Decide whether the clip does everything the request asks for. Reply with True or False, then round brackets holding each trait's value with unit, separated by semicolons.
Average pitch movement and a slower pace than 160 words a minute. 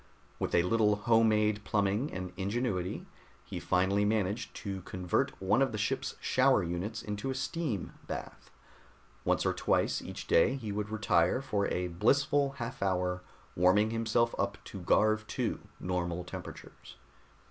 True (3.7 semitones; 150 wpm)